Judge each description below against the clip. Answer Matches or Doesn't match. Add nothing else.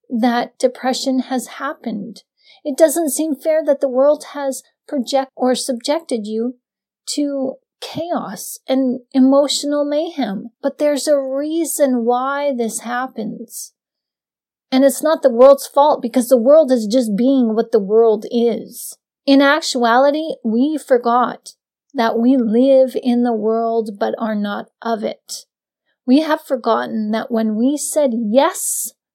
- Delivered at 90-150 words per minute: Matches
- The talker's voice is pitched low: Doesn't match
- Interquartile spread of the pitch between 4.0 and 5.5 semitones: Doesn't match